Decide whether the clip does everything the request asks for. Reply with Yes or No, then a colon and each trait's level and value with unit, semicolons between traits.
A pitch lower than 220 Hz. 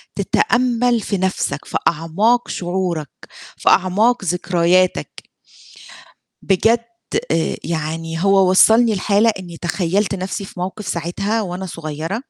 Yes: medium, 185 Hz